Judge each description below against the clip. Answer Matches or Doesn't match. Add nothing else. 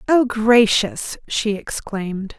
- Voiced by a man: Doesn't match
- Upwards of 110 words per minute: Doesn't match